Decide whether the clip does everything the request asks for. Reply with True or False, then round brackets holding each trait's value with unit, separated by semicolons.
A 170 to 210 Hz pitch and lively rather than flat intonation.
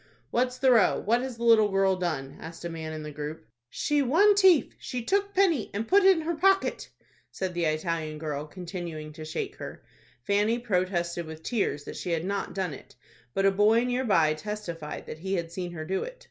True (190 Hz; 7.2 semitones)